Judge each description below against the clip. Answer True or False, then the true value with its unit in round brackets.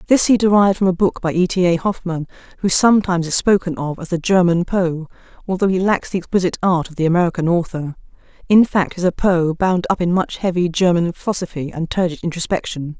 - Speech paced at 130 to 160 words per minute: False (205 wpm)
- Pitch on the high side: False (180 Hz)